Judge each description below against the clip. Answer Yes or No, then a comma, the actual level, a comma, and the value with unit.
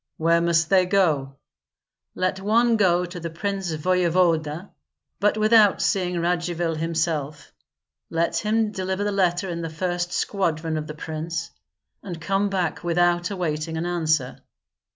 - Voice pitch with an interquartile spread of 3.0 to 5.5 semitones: No, narrow, 2.6 semitones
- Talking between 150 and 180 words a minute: No, average, 140 wpm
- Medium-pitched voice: Yes, medium, 175 Hz